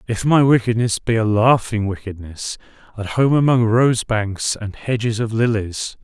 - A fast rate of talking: No, average, 160 wpm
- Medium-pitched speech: No, low, 115 Hz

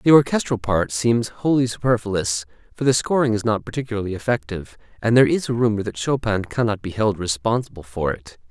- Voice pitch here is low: Yes, low, 110 Hz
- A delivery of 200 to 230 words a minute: No, average, 185 wpm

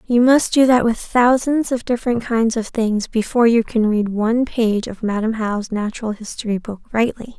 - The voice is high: Yes, high, 230 Hz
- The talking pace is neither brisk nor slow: Yes, average, 195 wpm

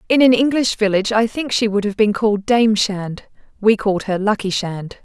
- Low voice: No, high, 215 Hz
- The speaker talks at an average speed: No, fast, 215 wpm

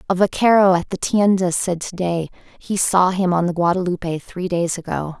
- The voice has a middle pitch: Yes, medium, 180 Hz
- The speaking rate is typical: Yes, average, 195 wpm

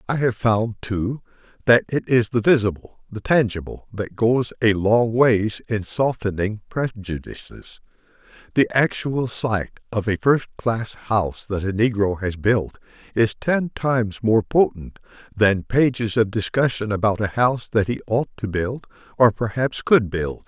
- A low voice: Yes, low, 110 Hz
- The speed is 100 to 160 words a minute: Yes, average, 150 wpm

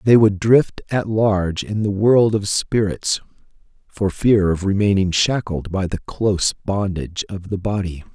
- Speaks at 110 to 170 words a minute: Yes, average, 160 wpm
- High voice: No, low, 100 Hz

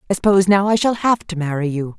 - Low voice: No, medium, 185 Hz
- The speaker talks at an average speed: No, fast, 270 wpm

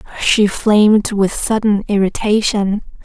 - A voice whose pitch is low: No, high, 210 Hz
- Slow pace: Yes, slow, 100 wpm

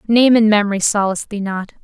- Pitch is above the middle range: Yes, high, 210 Hz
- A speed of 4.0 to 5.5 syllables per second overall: No, 6.4 syllables/s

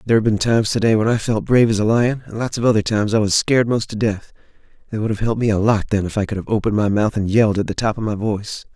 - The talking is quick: Yes, fast, 315 wpm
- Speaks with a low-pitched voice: Yes, low, 110 Hz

